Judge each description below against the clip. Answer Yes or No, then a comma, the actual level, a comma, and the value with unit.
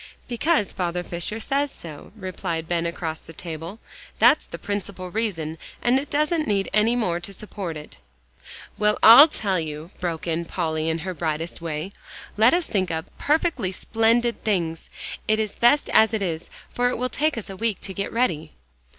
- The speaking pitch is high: Yes, high, 195 Hz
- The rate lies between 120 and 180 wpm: Yes, average, 175 wpm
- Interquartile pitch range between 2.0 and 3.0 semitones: No, wide, 5.6 semitones